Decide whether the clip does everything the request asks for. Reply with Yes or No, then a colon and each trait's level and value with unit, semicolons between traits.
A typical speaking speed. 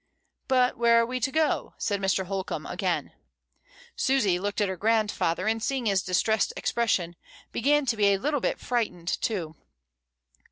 Yes: average, 160 wpm